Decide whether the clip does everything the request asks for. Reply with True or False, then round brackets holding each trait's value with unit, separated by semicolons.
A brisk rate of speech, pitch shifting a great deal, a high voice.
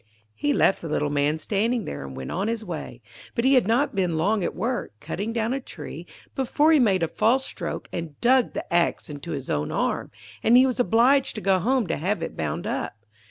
True (225 wpm; 7.4 semitones; 200 Hz)